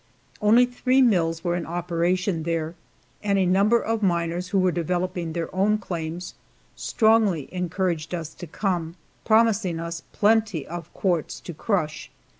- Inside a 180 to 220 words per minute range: No, average, 145 wpm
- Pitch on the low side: No, medium, 180 Hz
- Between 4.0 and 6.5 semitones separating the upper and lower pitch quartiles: No, average, 3.6 semitones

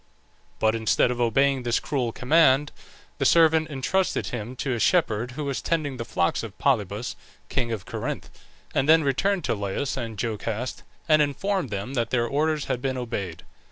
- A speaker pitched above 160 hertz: No, low, 125 Hz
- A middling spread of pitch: Yes, average, 4.4 semitones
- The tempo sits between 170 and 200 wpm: Yes, average, 175 wpm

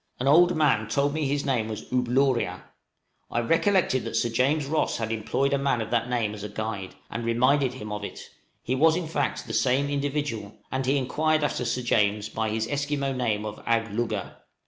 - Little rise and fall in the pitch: No, average, 4.2 semitones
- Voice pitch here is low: Yes, low, 125 Hz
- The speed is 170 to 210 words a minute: Yes, average, 200 wpm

